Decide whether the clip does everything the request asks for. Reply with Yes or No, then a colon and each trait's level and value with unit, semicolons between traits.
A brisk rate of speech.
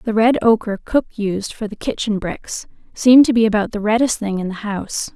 Yes: fast, 220 wpm